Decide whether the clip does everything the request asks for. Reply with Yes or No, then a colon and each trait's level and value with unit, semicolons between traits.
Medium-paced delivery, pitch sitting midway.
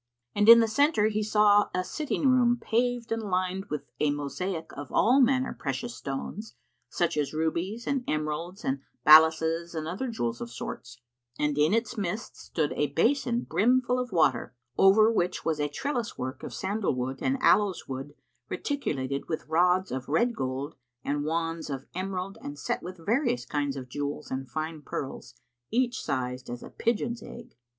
Yes: average, 170 wpm; medium, 175 Hz